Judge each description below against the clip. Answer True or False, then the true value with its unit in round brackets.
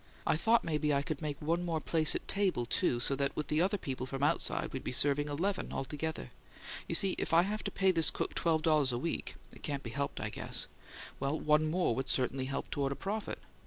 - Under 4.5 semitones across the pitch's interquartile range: True (3.6 semitones)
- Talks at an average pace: False (235 wpm)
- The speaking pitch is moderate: True (150 Hz)